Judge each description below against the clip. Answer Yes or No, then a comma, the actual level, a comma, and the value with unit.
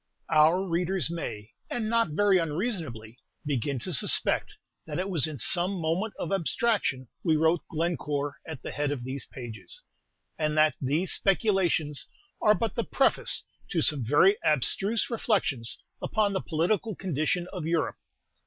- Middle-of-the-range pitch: Yes, medium, 165 Hz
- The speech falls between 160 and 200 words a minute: No, average, 150 wpm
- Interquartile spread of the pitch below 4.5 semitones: No, average, 4.9 semitones